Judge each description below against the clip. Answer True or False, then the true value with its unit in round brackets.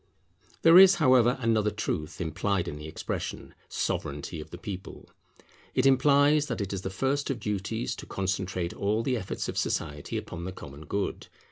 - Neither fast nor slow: True (170 wpm)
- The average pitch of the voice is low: True (100 Hz)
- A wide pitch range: True (6.4 semitones)